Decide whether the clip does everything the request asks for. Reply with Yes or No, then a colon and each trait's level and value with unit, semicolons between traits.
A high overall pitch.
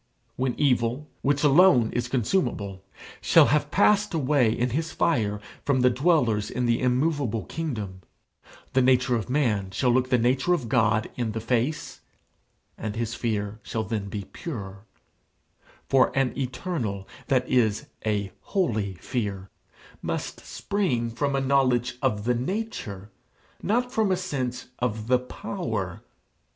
No: low, 125 Hz